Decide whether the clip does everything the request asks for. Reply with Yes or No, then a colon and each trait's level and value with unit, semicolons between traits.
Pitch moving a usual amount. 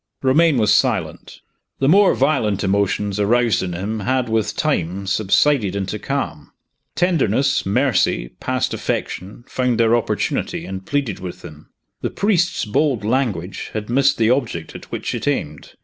No: wide, 5.8 semitones